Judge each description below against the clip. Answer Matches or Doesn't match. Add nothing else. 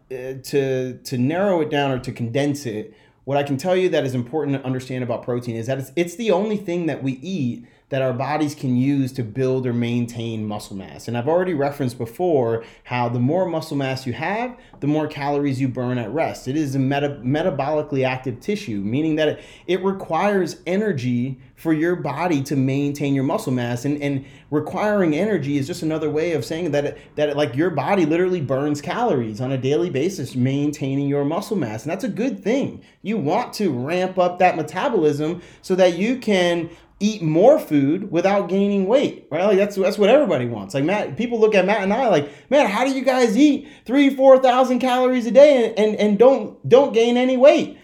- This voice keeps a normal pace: Doesn't match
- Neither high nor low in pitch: Matches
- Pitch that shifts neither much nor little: Doesn't match